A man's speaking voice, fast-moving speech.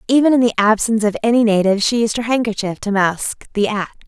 No: female; fast, 220 wpm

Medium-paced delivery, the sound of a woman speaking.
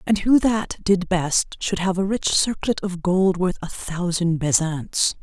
Yes: average, 185 wpm; female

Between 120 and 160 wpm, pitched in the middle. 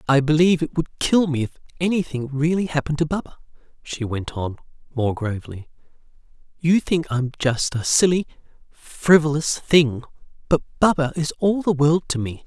Yes: average, 155 wpm; medium, 150 Hz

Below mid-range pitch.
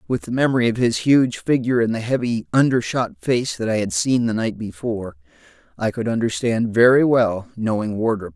Yes: low, 115 Hz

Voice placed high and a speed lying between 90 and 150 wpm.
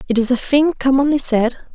No: very high, 260 Hz; fast, 205 wpm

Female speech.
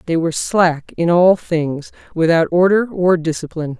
Yes: female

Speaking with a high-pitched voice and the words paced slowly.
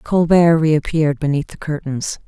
No: medium, 155 Hz; slow, 130 wpm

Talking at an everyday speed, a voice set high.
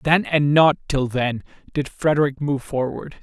No: average, 165 wpm; medium, 140 Hz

